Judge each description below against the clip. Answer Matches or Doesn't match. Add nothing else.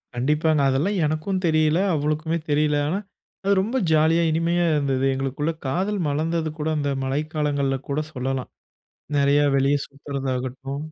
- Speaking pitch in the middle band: Matches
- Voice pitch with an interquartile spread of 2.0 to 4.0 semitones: Matches